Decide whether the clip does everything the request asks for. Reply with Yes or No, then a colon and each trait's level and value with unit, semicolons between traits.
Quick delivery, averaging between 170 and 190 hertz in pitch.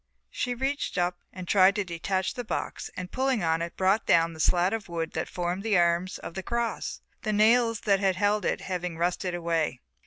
Yes: fast, 210 wpm; medium, 185 Hz